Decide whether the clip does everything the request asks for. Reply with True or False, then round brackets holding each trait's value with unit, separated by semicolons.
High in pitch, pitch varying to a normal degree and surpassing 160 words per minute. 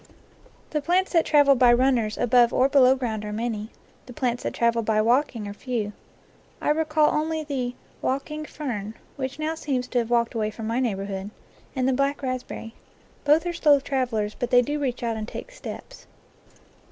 True (250 Hz; 4.1 semitones; 190 wpm)